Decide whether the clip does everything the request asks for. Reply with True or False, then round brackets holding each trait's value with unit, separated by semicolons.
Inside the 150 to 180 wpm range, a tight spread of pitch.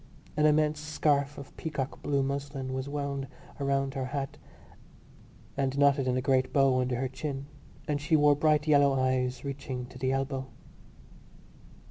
True (155 wpm; 1.7 semitones)